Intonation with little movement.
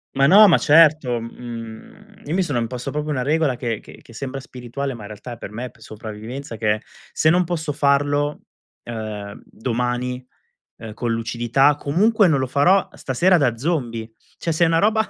No: average, 5.1 semitones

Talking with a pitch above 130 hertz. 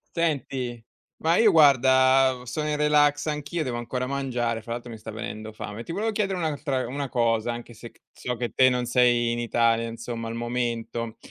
No: low, 125 Hz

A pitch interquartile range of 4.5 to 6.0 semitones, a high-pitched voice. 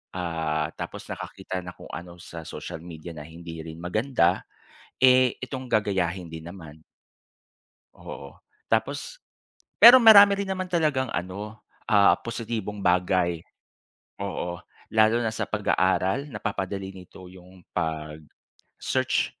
No: average, 4.9 semitones; very low, 95 Hz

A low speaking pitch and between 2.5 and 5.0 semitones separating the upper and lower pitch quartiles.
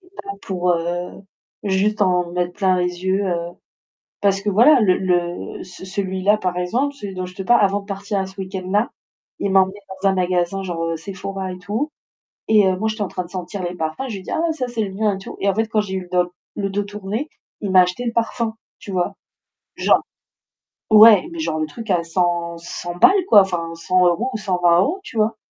No: high, 190 Hz; average, 2.8 semitones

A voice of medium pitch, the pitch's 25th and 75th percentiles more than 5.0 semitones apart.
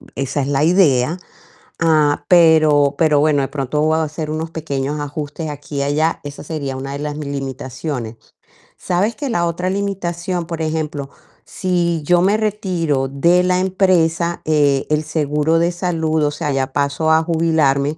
No: medium, 155 Hz; average, 3.0 semitones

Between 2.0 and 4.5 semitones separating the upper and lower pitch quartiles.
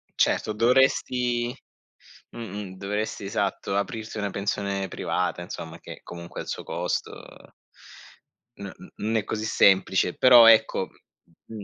Yes: average, 2.8 semitones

